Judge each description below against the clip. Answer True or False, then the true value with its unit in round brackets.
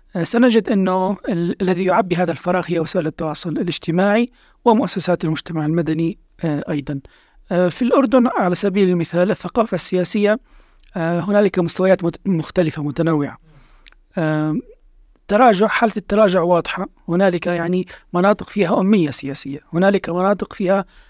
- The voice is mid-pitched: True (180 Hz)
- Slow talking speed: False (130 wpm)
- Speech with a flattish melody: False (3.5 semitones)